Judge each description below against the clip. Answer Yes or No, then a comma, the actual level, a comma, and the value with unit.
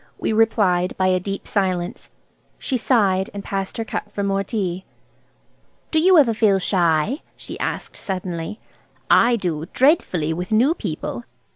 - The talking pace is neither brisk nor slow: Yes, average, 150 wpm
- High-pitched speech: Yes, high, 195 Hz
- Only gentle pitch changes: No, average, 3.9 semitones